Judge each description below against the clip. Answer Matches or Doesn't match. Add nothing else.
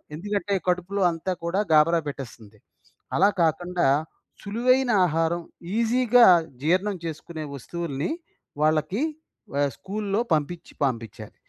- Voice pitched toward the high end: Doesn't match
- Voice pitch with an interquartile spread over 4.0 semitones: Matches